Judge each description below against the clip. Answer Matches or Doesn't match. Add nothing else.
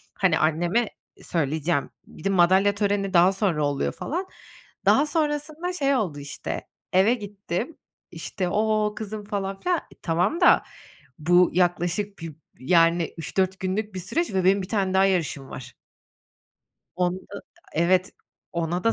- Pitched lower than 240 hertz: Matches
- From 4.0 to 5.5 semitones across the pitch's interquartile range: Doesn't match